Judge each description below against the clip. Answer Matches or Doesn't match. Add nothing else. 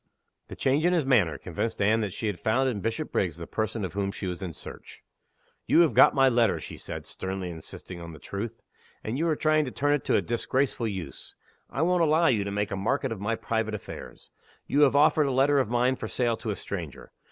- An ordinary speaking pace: Doesn't match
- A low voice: Matches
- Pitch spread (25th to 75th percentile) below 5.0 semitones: Doesn't match